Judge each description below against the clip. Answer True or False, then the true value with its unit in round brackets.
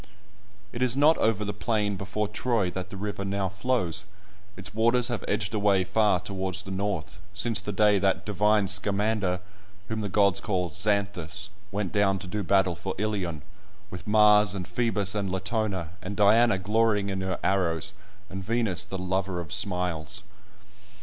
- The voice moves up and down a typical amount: False (2.1 semitones)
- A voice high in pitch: False (100 Hz)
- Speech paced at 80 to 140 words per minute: False (165 wpm)